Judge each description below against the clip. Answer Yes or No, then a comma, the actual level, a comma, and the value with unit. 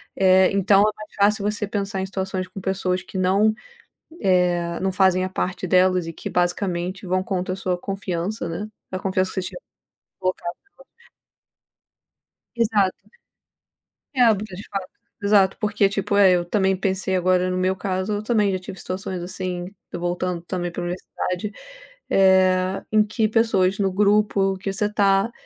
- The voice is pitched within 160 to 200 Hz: Yes, high, 190 Hz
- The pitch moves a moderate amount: No, narrow, 1.7 semitones